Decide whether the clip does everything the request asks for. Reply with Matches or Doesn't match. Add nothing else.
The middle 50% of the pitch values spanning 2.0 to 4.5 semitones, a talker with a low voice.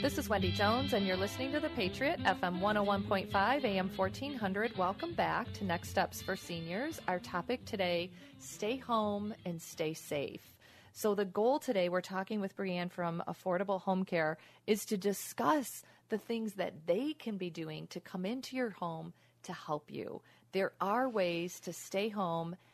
Doesn't match